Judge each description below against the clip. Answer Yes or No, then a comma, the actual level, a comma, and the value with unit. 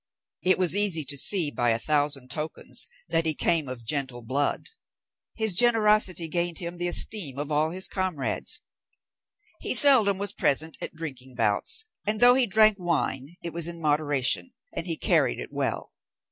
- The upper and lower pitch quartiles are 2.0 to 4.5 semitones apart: No, average, 5.3 semitones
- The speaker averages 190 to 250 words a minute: No, average, 170 wpm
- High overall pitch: No, medium, 165 Hz